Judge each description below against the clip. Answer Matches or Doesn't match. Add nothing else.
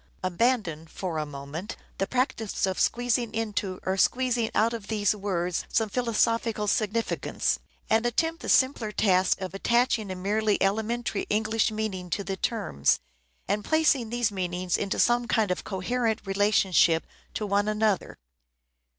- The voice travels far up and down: Doesn't match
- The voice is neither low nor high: Doesn't match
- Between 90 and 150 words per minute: Matches